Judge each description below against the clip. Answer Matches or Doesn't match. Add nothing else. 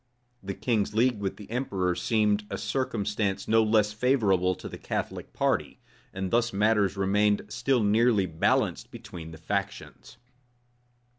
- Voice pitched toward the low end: Matches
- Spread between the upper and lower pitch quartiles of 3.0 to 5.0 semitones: Doesn't match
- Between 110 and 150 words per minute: Matches